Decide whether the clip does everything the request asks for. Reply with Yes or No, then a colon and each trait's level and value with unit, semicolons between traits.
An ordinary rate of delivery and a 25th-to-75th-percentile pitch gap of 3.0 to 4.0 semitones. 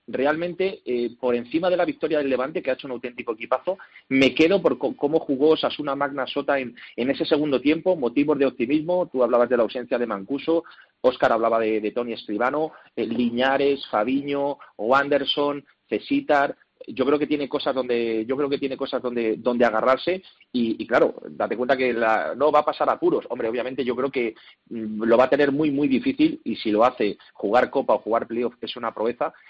No: fast, 205 wpm; average, 3.6 semitones